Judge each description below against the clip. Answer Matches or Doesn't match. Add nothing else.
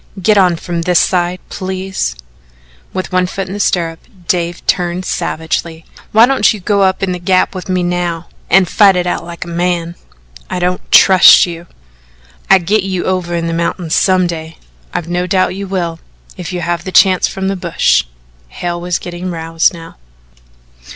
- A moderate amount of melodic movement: Doesn't match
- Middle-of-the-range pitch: Matches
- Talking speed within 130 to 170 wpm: Doesn't match